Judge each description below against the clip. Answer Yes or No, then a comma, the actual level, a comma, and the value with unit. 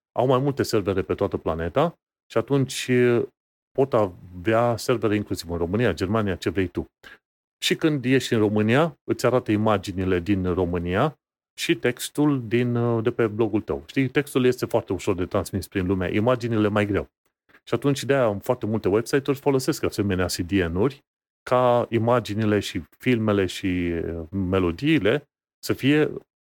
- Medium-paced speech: Yes, average, 150 wpm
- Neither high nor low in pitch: No, low, 115 Hz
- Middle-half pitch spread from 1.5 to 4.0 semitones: No, average, 4.7 semitones